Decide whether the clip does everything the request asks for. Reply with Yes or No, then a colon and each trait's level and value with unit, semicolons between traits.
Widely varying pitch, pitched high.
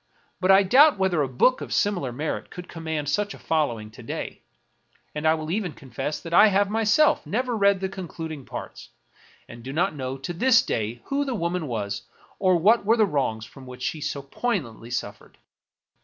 No: wide, 7.1 semitones; medium, 165 Hz